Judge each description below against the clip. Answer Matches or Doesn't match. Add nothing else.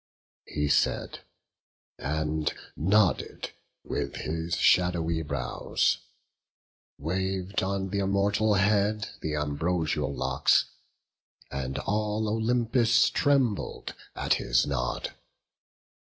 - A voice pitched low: Matches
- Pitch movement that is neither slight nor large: Doesn't match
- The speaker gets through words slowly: Matches